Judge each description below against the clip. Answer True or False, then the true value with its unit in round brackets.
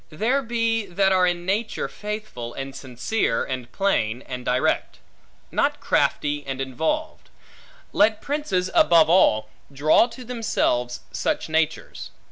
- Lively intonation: True (8.6 semitones)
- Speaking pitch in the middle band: True (175 Hz)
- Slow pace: True (125 wpm)